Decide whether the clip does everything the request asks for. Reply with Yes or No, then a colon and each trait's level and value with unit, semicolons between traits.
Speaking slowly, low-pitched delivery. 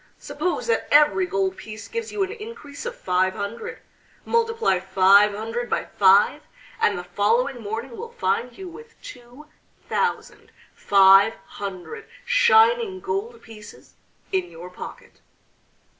No: slow, 130 wpm; very high, 255 Hz